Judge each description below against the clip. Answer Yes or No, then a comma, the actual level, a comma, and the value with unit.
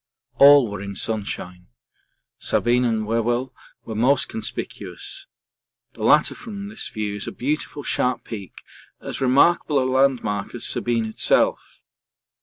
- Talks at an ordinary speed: No, slow, 130 wpm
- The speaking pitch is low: Yes, low, 120 Hz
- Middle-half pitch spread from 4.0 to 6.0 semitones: Yes, average, 4.6 semitones